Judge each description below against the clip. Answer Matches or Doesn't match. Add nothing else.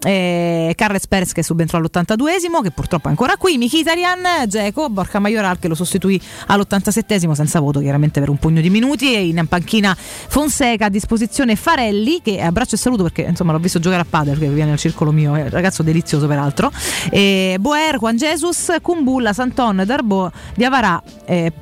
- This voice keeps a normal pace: Doesn't match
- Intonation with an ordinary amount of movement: Doesn't match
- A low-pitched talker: Doesn't match